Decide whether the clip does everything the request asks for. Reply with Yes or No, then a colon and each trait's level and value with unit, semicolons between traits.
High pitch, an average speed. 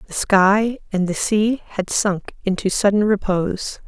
Yes: high, 205 Hz; average, 155 wpm